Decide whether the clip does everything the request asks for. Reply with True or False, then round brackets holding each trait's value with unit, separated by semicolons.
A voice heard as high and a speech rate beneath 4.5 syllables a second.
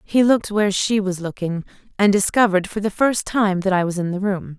False (195 Hz; 5.8 syllables/s)